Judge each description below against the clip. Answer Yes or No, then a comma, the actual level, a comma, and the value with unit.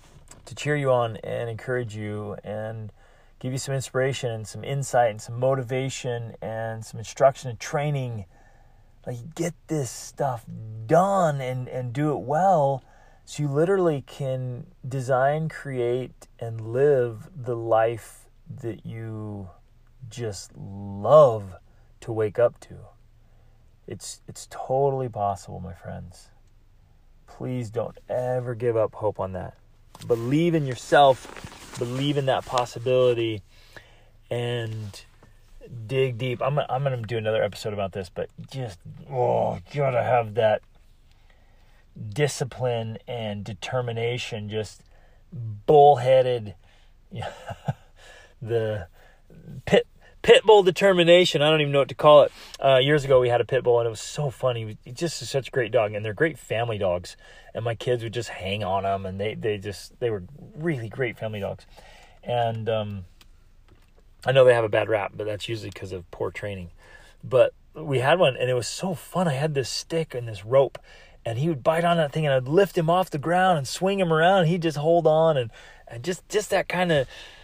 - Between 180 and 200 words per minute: No, average, 160 wpm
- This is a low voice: Yes, low, 120 Hz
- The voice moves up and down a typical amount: Yes, average, 4.3 semitones